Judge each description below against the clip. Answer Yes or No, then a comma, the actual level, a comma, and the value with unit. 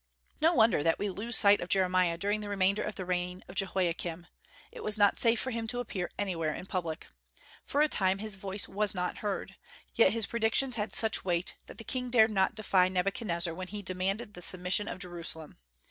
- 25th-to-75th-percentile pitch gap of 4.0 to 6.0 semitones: No, average, 3.2 semitones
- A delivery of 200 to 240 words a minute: Yes, fast, 205 wpm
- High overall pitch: Yes, high, 195 Hz